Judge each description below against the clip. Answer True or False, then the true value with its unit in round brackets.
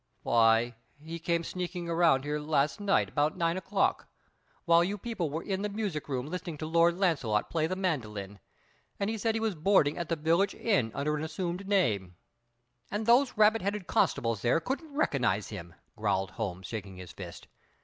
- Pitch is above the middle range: False (165 Hz)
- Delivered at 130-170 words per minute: False (185 wpm)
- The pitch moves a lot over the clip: True (8.1 semitones)